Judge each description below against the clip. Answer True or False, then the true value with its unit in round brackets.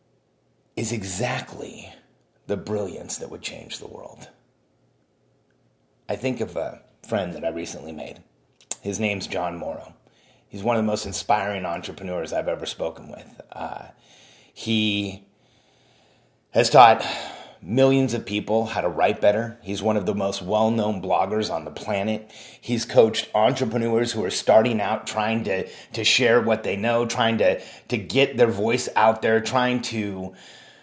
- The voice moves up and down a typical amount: True (3.0 semitones)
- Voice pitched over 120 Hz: False (110 Hz)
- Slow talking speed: False (155 wpm)